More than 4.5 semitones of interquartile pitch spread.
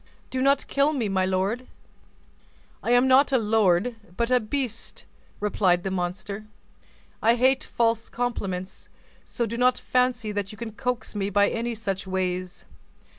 No: average, 4.2 semitones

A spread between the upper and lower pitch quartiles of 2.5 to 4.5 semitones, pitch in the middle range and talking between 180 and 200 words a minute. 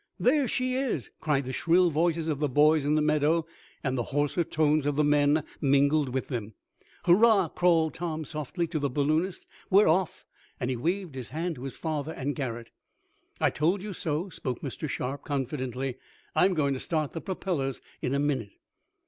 Yes: average, 3.6 semitones; medium, 150 Hz; average, 185 wpm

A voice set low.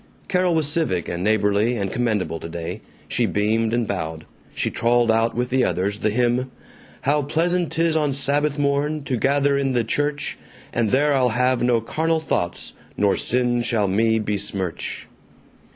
Yes: low, 120 Hz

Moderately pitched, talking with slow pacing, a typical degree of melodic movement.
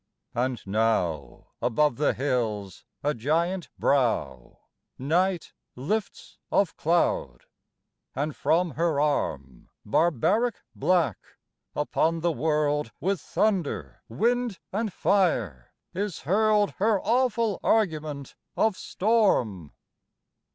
No: medium, 155 Hz; slow, 95 wpm; wide, 8.2 semitones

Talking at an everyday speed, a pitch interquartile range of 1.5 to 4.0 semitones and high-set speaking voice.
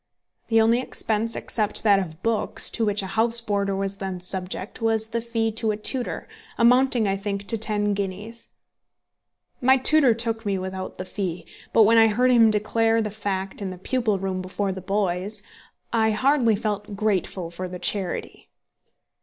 Yes: average, 175 wpm; average, 2.7 semitones; high, 210 Hz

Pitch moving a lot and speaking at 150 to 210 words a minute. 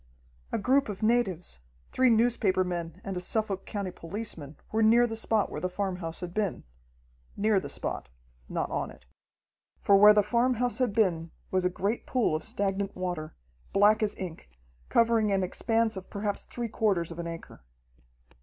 No: average, 3.6 semitones; average, 175 wpm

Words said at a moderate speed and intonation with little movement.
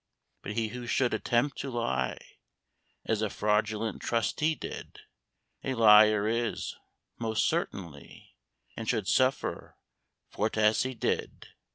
No: slow, 125 wpm; narrow, 2.1 semitones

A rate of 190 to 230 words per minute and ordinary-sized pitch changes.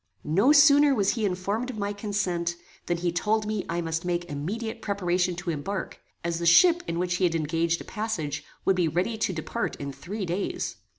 Yes: average, 200 wpm; average, 3.8 semitones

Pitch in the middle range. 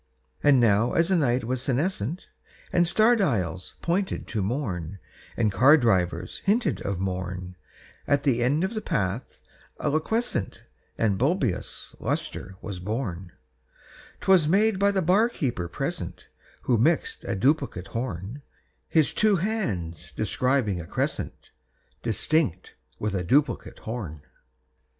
No: low, 125 Hz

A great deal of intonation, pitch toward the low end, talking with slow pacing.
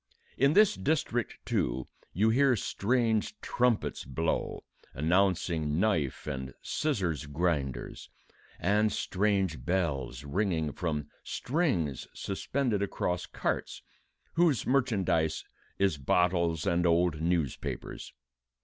Yes: wide, 6.0 semitones; very low, 90 Hz; slow, 95 wpm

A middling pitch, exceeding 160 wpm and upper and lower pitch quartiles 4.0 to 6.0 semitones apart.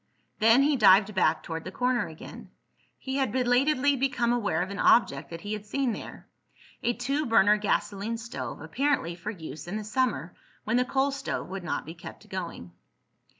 No: high, 220 Hz; average, 180 wpm; wide, 5.6 semitones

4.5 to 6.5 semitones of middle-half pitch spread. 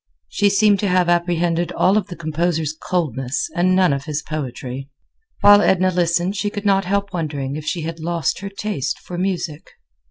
No: average, 3.8 semitones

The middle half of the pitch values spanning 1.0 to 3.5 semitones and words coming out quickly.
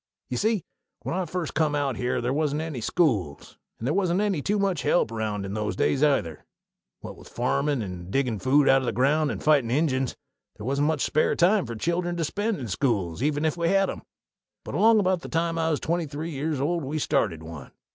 No: wide, 5.5 semitones; fast, 225 wpm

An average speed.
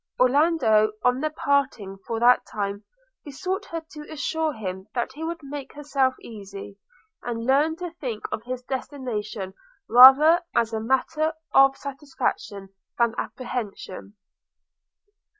No: slow, 130 wpm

